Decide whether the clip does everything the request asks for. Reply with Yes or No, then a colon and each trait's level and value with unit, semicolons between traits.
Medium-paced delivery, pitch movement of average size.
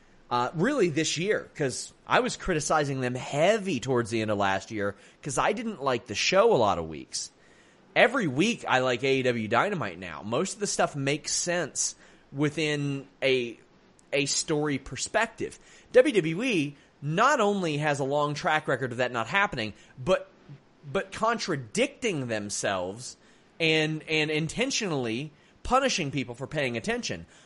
No: average, 150 wpm; wide, 6.2 semitones